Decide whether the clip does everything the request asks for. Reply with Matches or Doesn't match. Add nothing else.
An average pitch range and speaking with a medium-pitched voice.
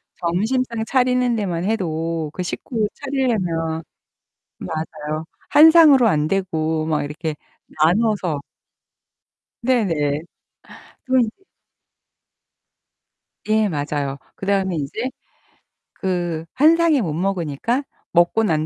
Doesn't match